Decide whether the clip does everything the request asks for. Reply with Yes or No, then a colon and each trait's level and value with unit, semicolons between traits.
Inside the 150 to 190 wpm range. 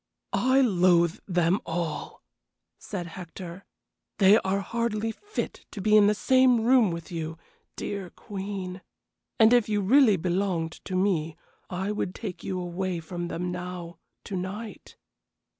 No: average, 140 wpm